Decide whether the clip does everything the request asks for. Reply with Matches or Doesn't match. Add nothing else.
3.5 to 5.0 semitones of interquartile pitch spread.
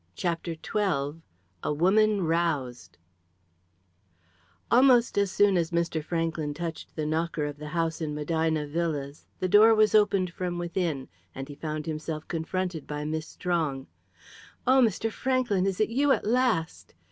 Matches